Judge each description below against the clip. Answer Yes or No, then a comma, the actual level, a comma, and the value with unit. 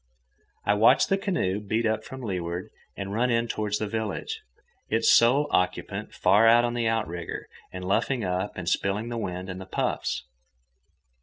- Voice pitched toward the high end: No, low, 105 Hz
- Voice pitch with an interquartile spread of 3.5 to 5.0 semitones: Yes, average, 4.0 semitones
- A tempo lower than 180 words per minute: Yes, average, 170 wpm